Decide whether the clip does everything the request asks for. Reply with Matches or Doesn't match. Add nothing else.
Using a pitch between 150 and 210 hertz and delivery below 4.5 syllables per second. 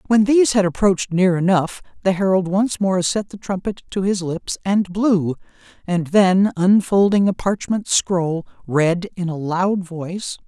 Matches